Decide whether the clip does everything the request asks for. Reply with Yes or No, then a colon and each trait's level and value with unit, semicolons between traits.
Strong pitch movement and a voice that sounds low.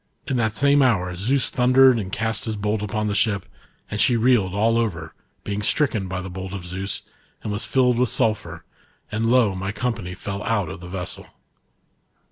No: average, 3.8 semitones; low, 105 Hz